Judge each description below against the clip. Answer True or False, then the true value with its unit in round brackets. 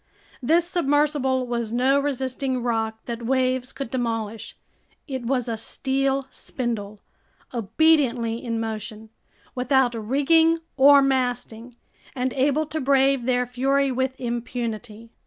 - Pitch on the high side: True (255 Hz)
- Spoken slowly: True (120 wpm)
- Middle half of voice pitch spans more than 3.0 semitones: False (2.7 semitones)